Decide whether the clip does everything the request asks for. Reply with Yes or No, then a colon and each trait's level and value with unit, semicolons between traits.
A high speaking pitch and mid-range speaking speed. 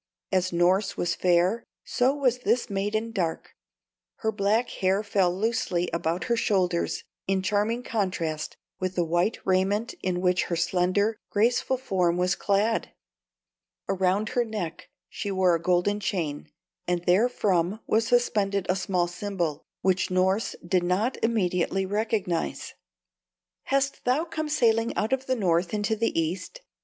Yes: high, 195 Hz; average, 145 wpm